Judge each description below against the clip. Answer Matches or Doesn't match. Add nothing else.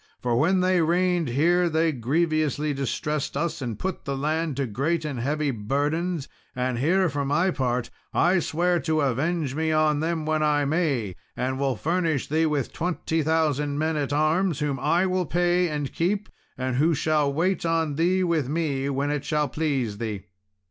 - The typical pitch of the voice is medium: Matches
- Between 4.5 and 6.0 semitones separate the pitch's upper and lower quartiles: Doesn't match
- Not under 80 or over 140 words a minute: Doesn't match